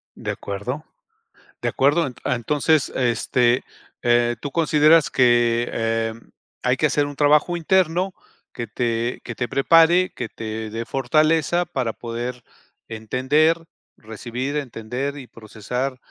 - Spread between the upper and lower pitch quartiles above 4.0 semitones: Yes, average, 4.4 semitones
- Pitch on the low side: Yes, low, 125 Hz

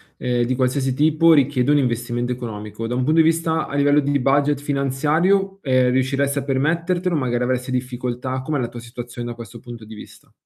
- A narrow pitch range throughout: No, average, 3.1 semitones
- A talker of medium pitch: No, low, 130 Hz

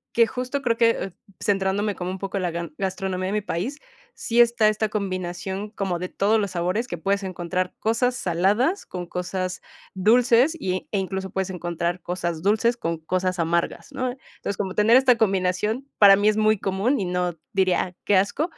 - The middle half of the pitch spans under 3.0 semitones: No, average, 3.3 semitones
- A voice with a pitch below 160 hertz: No, high, 195 Hz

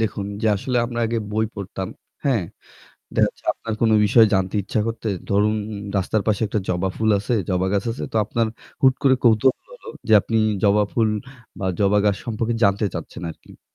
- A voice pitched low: Yes, low, 110 Hz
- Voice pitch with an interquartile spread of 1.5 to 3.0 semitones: Yes, narrow, 2.6 semitones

